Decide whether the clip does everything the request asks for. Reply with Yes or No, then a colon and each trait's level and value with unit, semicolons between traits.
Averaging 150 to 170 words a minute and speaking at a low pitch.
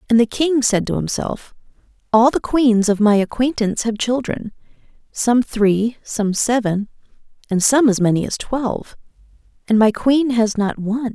No: average, 160 wpm; high, 230 Hz